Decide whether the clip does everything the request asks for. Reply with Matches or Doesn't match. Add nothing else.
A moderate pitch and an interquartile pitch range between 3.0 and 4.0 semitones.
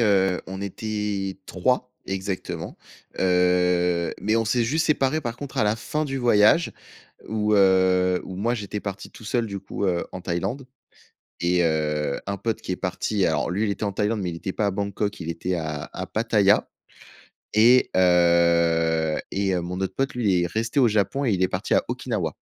Doesn't match